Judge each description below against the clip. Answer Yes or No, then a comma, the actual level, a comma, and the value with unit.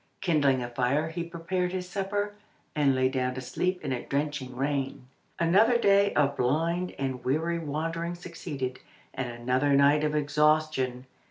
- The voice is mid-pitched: Yes, medium, 150 Hz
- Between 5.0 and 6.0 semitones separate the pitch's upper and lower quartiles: No, average, 4.4 semitones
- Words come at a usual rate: Yes, average, 155 wpm